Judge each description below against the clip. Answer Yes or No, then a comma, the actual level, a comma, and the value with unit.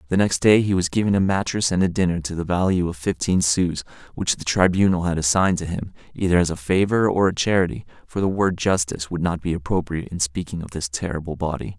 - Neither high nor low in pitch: No, very low, 90 Hz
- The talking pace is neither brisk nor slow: No, fast, 230 wpm